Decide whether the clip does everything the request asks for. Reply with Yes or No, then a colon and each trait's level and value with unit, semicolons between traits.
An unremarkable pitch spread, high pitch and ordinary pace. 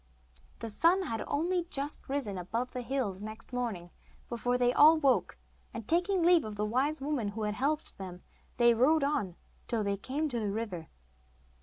No: wide, 5.8 semitones; high, 245 Hz; average, 180 wpm